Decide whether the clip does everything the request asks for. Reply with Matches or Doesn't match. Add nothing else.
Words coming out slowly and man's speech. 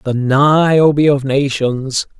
Matches